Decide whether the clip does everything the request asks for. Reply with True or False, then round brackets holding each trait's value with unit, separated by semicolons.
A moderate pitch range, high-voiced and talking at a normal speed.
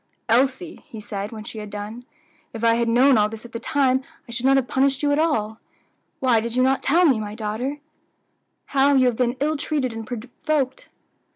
False (3.4 semitones; 250 Hz; 210 wpm)